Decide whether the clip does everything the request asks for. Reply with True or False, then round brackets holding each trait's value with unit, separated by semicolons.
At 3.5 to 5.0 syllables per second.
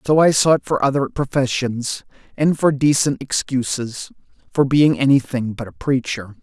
True (4.5 syllables/s)